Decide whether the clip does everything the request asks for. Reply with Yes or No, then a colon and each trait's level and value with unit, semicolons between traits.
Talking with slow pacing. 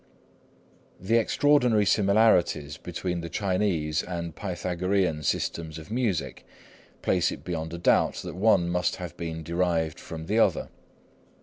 Yes: slow, 130 wpm